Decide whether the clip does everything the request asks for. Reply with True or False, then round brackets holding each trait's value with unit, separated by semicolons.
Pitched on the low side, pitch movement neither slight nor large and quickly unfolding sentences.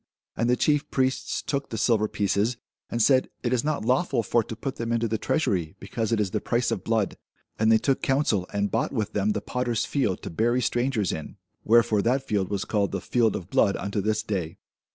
True (115 Hz; 3.4 semitones; 220 wpm)